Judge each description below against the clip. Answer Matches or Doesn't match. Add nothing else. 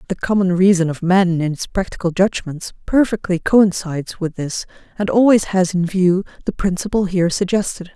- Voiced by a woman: Matches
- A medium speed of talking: Matches